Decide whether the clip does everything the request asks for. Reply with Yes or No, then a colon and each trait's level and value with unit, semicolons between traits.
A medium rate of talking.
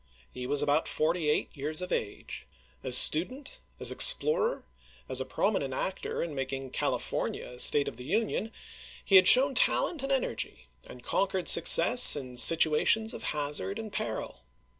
Yes: average, 160 wpm